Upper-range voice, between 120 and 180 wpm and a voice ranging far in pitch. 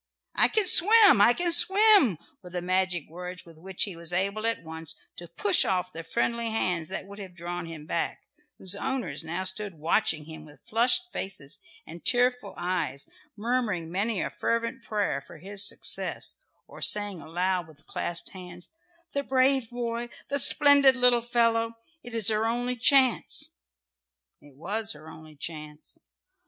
Yes: high, 195 Hz; average, 165 wpm; wide, 6.0 semitones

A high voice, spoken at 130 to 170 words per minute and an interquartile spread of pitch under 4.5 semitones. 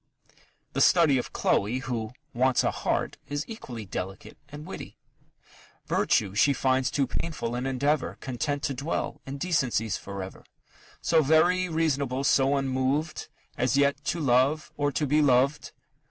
No: low, 135 Hz; average, 155 wpm; average, 3.0 semitones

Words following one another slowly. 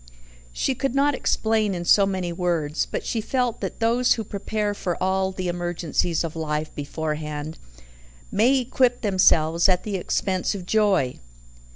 No: average, 155 wpm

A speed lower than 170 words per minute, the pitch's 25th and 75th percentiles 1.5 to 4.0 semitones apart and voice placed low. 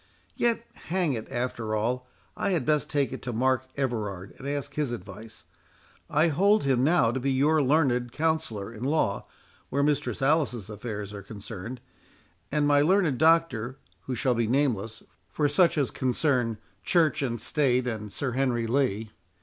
No: average, 160 wpm; average, 4.5 semitones; low, 130 Hz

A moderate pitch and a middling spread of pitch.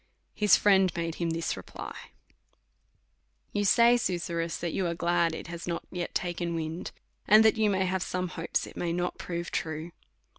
No: medium, 175 Hz; narrow, 2.0 semitones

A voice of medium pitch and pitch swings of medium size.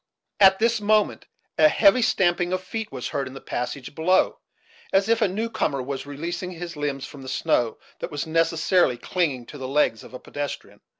No: medium, 165 Hz; wide, 5.7 semitones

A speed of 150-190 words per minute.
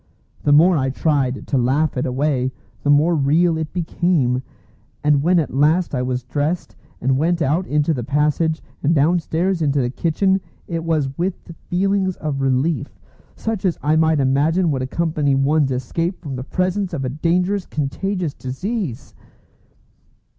Yes: average, 160 wpm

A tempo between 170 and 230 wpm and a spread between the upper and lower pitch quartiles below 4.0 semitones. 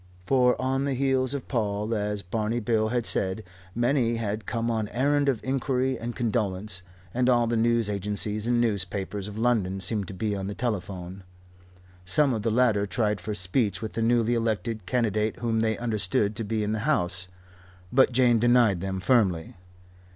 Yes: average, 180 wpm; average, 3.0 semitones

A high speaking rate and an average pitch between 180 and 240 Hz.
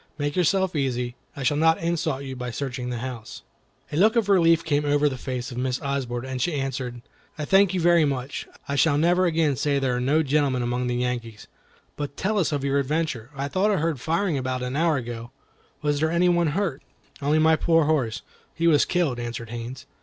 No: fast, 220 wpm; medium, 140 Hz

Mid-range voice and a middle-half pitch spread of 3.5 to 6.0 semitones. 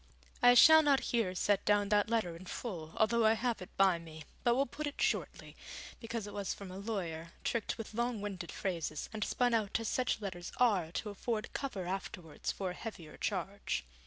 No: high, 205 Hz; average, 4.2 semitones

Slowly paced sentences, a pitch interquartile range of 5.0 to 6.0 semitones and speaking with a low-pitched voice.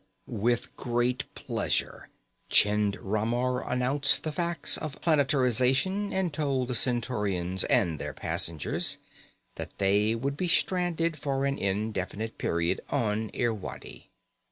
Yes: slow, 115 wpm; average, 5.3 semitones; low, 125 Hz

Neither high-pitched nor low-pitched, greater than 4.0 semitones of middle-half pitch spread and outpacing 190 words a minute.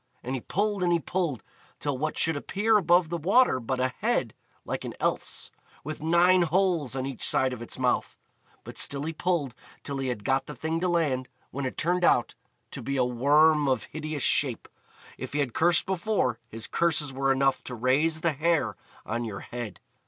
Yes: medium, 145 Hz; average, 4.8 semitones; average, 200 wpm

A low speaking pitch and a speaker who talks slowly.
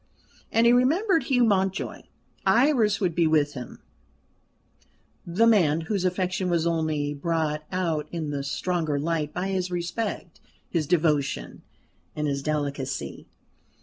No: medium, 170 Hz; slow, 130 wpm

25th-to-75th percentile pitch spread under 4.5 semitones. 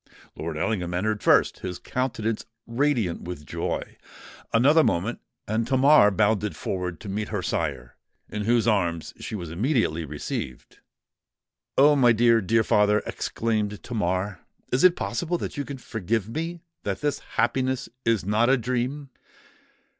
No: average, 5.3 semitones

